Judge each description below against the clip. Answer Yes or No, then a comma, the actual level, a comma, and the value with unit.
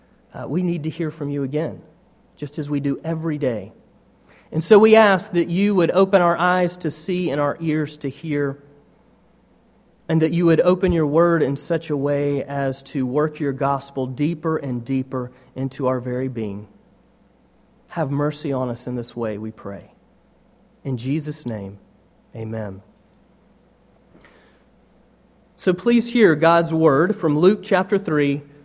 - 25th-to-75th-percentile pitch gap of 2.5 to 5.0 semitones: Yes, average, 4.2 semitones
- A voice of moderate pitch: Yes, medium, 150 Hz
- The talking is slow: No, average, 160 wpm